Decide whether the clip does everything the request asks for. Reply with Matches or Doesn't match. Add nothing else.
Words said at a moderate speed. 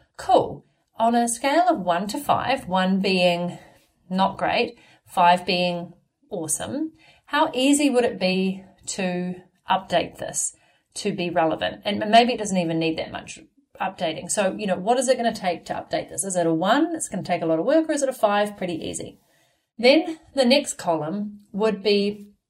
Matches